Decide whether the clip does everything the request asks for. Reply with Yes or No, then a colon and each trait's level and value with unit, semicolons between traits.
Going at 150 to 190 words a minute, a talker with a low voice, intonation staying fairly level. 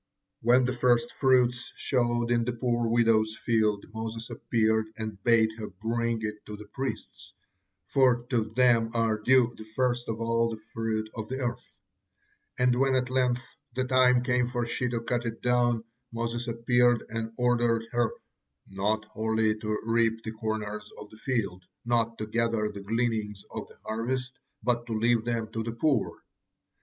Yes: average, 170 wpm; low, 115 Hz; narrow, 1.8 semitones